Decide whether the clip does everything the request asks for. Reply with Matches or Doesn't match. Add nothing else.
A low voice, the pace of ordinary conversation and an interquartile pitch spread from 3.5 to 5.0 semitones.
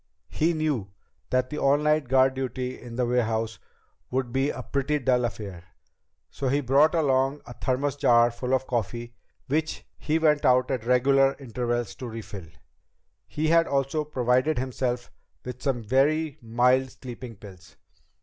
Doesn't match